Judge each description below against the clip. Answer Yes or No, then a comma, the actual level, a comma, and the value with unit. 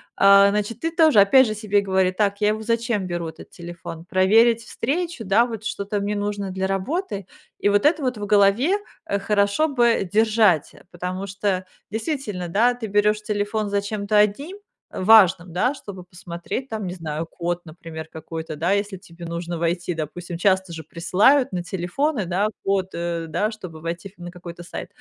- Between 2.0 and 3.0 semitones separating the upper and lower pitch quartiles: No, average, 3.7 semitones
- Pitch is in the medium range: No, high, 200 Hz